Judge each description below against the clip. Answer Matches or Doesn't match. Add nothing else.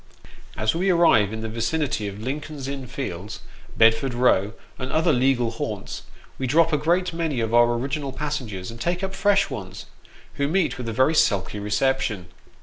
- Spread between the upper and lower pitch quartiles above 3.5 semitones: Matches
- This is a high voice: Doesn't match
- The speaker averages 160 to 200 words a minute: Matches